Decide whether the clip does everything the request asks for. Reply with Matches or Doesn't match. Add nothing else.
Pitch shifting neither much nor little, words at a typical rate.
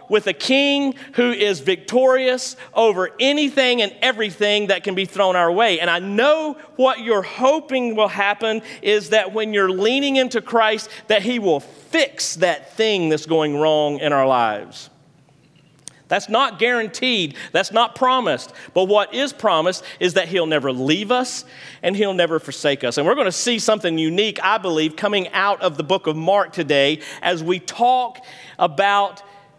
Doesn't match